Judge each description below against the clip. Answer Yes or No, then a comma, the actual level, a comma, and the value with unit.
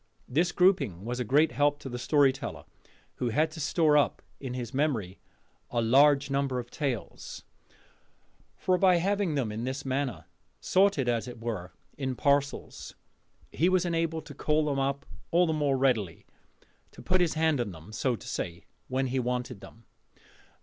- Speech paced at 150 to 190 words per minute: Yes, average, 170 wpm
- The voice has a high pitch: No, low, 135 Hz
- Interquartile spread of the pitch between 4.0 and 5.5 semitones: Yes, average, 4.3 semitones